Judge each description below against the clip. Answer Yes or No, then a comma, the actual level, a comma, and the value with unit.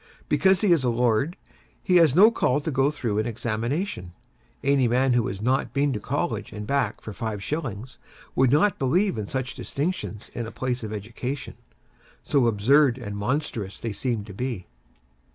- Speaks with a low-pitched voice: Yes, low, 125 Hz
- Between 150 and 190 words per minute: Yes, average, 185 wpm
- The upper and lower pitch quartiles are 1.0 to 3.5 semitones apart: No, average, 4.5 semitones